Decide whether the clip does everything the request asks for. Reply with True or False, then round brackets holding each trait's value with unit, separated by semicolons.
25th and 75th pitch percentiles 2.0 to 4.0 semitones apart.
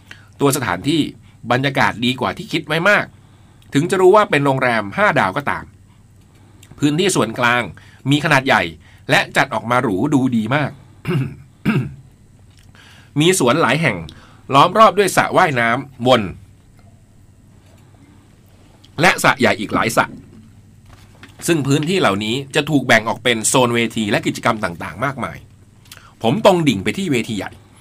False (4.7 semitones)